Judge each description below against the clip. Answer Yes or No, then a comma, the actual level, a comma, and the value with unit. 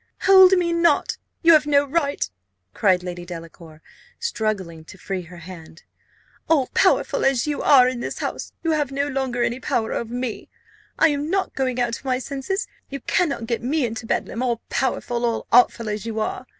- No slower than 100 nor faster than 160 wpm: No, average, 190 wpm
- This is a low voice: No, very high, 250 Hz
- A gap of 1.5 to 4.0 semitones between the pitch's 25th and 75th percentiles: No, average, 4.9 semitones